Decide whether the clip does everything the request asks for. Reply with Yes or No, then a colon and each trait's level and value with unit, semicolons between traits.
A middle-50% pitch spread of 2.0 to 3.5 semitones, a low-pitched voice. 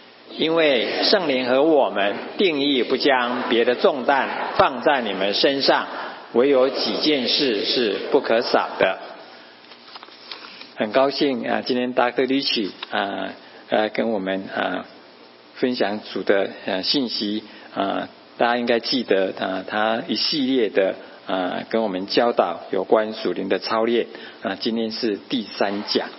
No: average, 4.8 semitones; low, 110 Hz